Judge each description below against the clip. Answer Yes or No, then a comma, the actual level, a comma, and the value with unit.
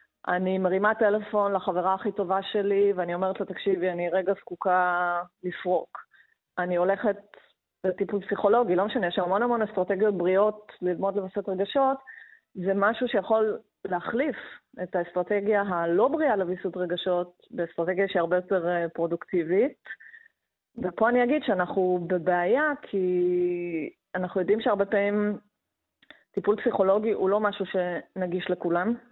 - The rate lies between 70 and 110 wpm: No, average, 125 wpm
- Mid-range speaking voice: No, high, 195 Hz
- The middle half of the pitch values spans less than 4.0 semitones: Yes, narrow, 2.5 semitones